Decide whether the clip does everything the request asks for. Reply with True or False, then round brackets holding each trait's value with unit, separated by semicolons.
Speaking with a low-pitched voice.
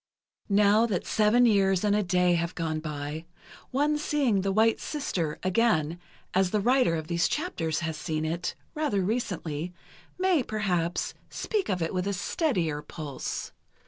False (185 Hz)